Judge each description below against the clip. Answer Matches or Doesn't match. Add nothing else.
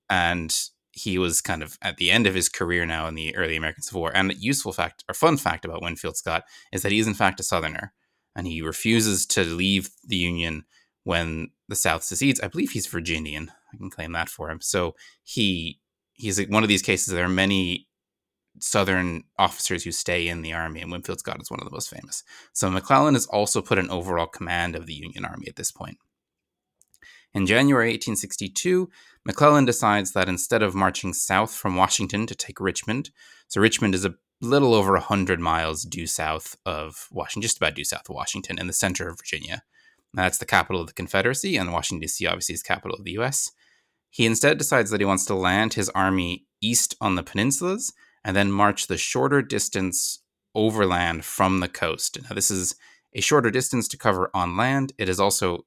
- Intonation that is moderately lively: Matches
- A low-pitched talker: Matches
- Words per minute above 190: Matches